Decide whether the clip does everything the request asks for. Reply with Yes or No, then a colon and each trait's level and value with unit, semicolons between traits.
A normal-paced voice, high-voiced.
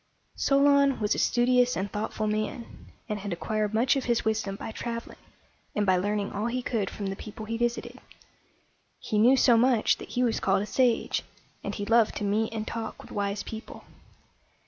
Yes: average, 190 wpm; high, 220 Hz